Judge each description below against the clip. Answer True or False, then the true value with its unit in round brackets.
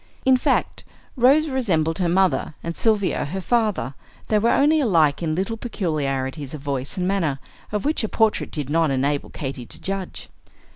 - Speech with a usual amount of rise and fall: False (7.2 semitones)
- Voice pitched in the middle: True (180 Hz)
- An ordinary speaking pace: True (175 wpm)